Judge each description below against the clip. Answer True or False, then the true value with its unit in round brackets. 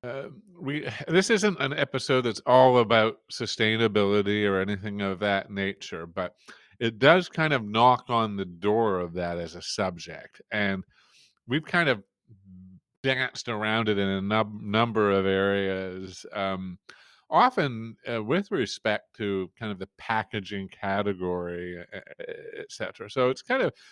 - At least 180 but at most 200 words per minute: False (150 wpm)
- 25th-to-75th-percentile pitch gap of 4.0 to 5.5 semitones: True (4.6 semitones)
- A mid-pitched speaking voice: False (105 Hz)